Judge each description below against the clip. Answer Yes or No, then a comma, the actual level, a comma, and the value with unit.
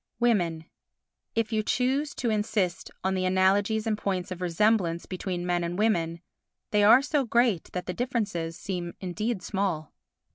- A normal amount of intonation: Yes, average, 3.9 semitones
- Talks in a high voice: Yes, high, 195 Hz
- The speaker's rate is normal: Yes, average, 155 wpm